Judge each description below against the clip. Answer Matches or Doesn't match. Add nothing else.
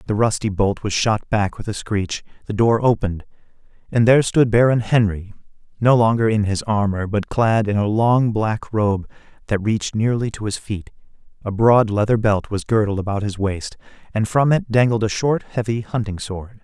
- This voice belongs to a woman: Doesn't match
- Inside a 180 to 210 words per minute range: Matches